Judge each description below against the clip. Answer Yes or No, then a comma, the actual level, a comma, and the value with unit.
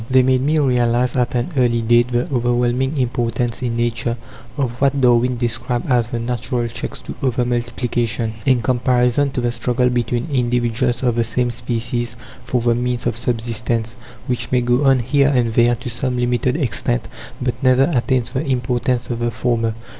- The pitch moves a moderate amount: No, narrow, 1.2 semitones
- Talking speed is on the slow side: No, average, 175 wpm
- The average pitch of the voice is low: Yes, low, 120 Hz